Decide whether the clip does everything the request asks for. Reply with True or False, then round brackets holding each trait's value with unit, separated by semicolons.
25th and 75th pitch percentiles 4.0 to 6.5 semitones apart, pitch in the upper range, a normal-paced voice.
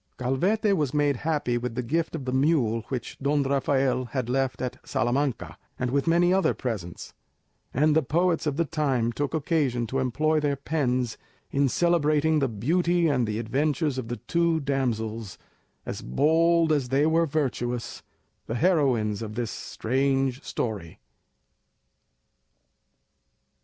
False (4.3 semitones; 135 Hz; 145 wpm)